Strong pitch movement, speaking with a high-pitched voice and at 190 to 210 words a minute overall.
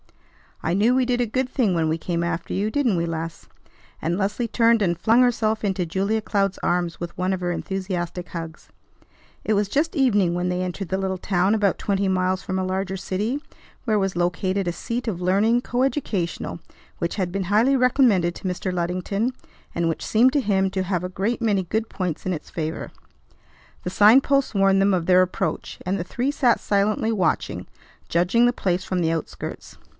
No: average, 3.8 semitones; high, 195 Hz; average, 200 wpm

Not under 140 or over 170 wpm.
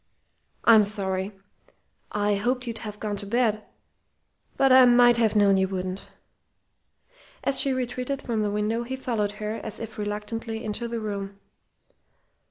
Yes: average, 150 wpm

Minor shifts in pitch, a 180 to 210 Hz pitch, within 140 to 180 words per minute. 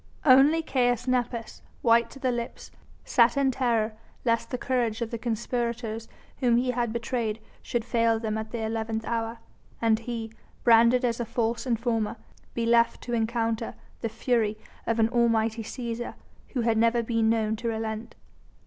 No: narrow, 1.3 semitones; high, 230 Hz; average, 165 wpm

